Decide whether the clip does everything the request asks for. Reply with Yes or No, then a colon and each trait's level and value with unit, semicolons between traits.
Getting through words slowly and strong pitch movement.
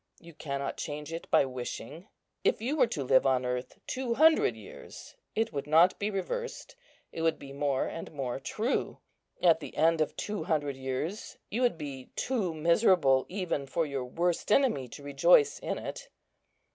No: average, 175 wpm; wide, 6.5 semitones